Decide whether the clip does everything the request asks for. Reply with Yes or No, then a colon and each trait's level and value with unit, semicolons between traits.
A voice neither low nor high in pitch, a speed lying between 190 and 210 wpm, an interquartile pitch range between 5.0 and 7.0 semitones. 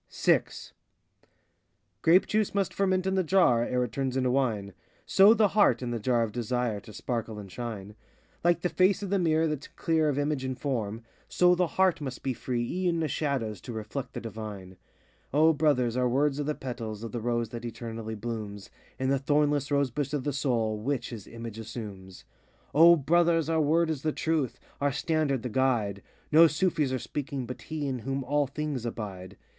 No: low, 130 Hz; average, 200 wpm; average, 5.3 semitones